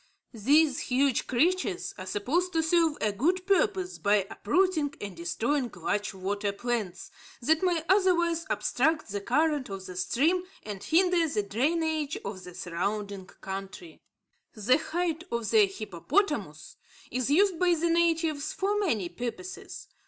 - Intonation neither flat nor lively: No, wide, 8.8 semitones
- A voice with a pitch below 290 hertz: No, very high, 295 Hz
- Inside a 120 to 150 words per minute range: Yes, average, 140 wpm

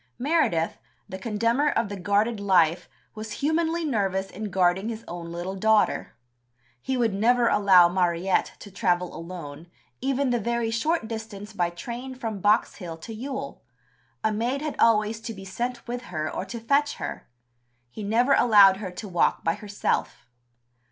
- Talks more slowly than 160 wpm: No, average, 165 wpm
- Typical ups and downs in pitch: Yes, average, 4.2 semitones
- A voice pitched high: Yes, high, 215 Hz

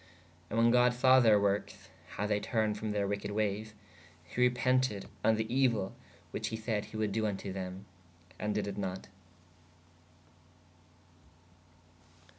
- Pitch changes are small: Yes, narrow, 2.3 semitones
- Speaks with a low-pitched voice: Yes, low, 105 Hz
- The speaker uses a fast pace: No, average, 150 wpm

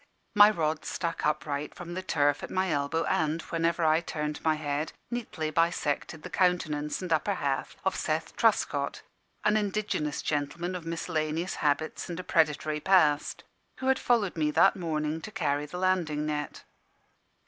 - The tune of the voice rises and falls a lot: No, average, 3.2 semitones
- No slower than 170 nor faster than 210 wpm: No, average, 160 wpm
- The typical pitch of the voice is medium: Yes, medium, 160 Hz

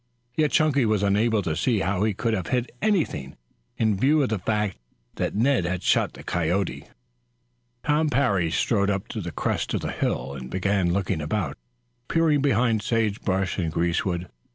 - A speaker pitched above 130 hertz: No, low, 105 Hz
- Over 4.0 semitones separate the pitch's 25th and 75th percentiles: Yes, average, 5.1 semitones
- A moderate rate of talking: Yes, average, 175 wpm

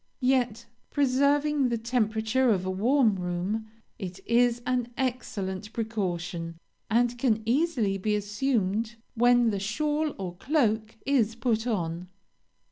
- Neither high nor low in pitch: No, high, 225 Hz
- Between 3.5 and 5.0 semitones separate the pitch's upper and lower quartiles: Yes, average, 4.0 semitones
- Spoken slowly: Yes, slow, 125 wpm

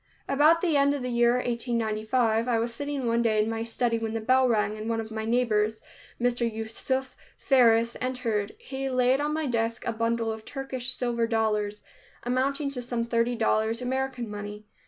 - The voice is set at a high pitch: Yes, high, 235 Hz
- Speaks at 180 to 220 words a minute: Yes, average, 185 wpm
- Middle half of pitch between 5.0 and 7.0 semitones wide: No, narrow, 2.4 semitones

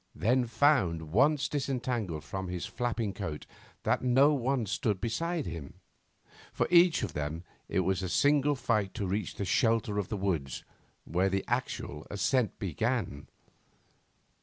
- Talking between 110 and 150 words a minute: Yes, average, 145 wpm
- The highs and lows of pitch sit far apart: Yes, wide, 5.9 semitones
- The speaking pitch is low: Yes, low, 110 Hz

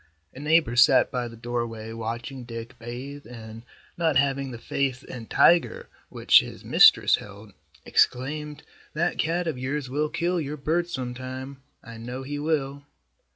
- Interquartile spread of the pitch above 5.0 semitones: No, average, 3.9 semitones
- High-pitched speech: No, low, 130 Hz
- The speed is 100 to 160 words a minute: Yes, average, 155 wpm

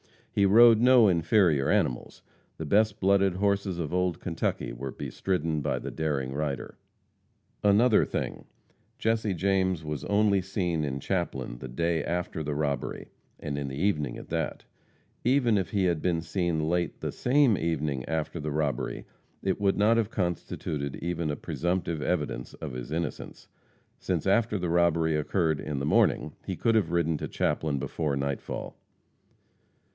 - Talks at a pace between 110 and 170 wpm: Yes, average, 160 wpm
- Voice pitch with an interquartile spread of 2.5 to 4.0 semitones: No, average, 4.7 semitones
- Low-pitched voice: Yes, very low, 85 Hz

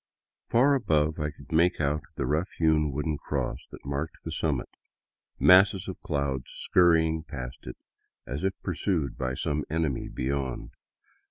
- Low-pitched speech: Yes, very low, 75 Hz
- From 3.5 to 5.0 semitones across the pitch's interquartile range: Yes, average, 3.8 semitones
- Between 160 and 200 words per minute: No, average, 150 wpm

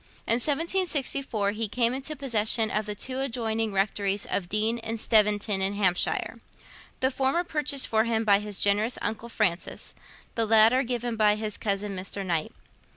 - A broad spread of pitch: No, average, 3.3 semitones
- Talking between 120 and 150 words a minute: No, average, 160 wpm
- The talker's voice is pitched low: No, high, 220 Hz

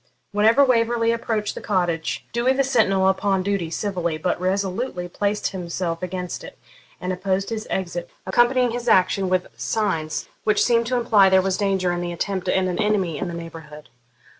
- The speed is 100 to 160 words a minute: No, average, 175 wpm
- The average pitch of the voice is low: No, high, 190 Hz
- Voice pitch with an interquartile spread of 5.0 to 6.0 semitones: No, average, 3.7 semitones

